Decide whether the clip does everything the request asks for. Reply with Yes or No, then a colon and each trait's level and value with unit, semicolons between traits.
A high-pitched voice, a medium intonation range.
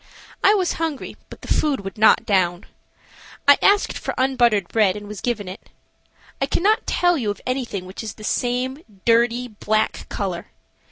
Yes: high, 230 Hz; average, 4.7 semitones